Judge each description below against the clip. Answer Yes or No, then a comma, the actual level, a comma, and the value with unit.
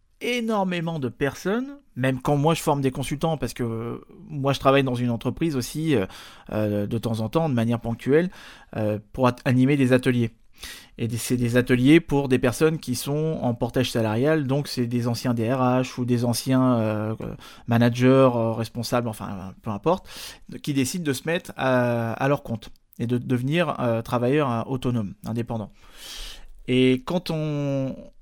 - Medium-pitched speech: No, low, 125 Hz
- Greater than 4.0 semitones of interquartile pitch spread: No, average, 3.6 semitones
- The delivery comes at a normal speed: Yes, average, 170 wpm